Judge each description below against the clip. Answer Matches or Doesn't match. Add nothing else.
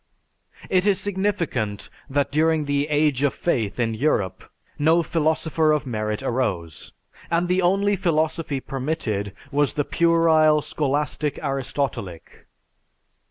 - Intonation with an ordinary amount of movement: Matches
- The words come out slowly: Matches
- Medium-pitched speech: Matches